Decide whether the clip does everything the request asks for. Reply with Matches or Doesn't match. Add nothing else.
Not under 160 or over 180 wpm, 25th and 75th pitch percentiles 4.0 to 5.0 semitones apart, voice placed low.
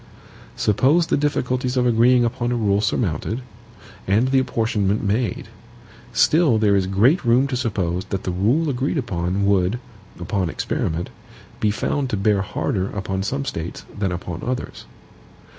Doesn't match